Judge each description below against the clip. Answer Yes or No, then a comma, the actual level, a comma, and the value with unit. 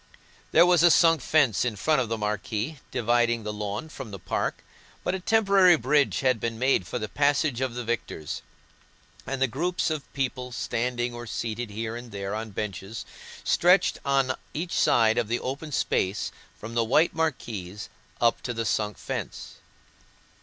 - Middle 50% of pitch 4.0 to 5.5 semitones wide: Yes, average, 4.8 semitones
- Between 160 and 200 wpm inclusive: Yes, average, 175 wpm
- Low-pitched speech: Yes, low, 120 Hz